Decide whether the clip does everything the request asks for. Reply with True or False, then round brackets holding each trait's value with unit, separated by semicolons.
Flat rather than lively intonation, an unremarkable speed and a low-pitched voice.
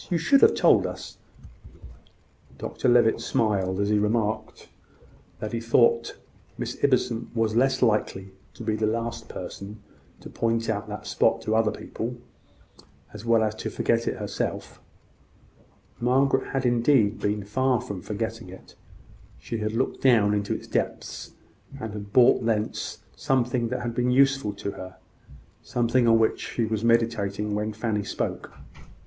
True (2.2 semitones; 150 wpm; 115 Hz)